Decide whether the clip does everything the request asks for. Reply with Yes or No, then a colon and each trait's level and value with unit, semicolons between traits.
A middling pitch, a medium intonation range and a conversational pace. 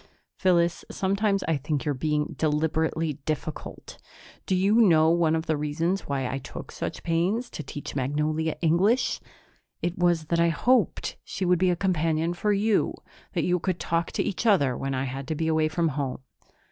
Yes: medium, 165 Hz; average, 3.2 semitones; average, 185 wpm